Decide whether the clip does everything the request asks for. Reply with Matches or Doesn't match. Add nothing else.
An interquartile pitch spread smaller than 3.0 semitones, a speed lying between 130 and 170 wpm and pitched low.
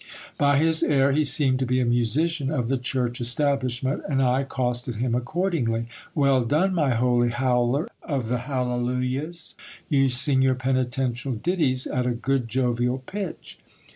Matches